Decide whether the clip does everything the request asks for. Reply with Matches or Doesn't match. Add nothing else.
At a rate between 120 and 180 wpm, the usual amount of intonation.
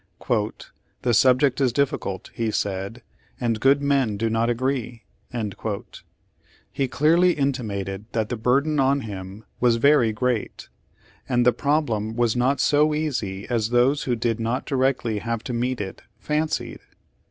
Matches